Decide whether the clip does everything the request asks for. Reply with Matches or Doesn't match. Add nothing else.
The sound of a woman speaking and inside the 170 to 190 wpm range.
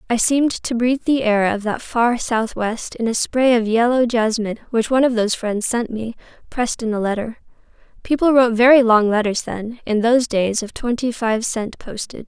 Doesn't match